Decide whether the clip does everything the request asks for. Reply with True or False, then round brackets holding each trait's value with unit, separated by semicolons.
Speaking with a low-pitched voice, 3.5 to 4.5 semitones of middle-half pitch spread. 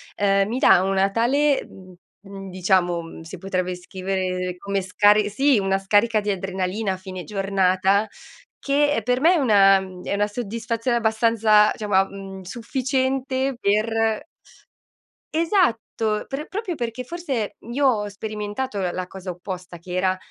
False (205 Hz; 3.8 semitones)